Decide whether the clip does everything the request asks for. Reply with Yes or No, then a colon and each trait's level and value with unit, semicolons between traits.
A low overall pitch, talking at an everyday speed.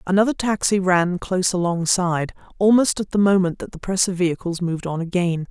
No: medium, 185 Hz; average, 185 wpm